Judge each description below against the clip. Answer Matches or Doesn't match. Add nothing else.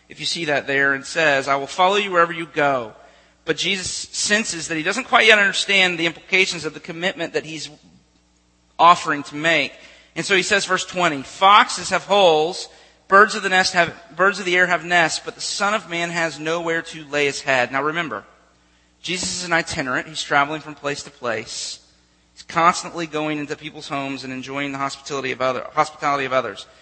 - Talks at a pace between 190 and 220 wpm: Matches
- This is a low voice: Doesn't match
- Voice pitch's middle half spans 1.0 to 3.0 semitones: Doesn't match